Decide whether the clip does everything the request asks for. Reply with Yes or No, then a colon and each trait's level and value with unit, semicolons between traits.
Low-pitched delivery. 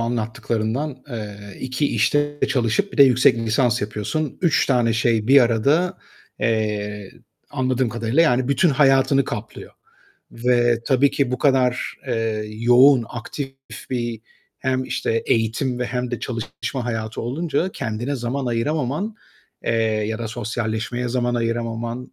Yes: low, 120 Hz